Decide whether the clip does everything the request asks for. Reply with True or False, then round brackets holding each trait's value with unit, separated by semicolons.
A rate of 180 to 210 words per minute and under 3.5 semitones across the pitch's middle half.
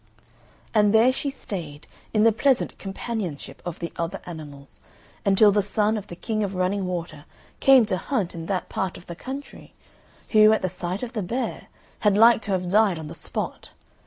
False (190 wpm; 3.9 semitones)